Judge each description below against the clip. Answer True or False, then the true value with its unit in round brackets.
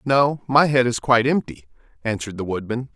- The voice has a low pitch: True (125 Hz)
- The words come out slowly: False (185 wpm)